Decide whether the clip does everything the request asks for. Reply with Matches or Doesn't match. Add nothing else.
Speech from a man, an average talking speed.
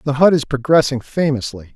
Matches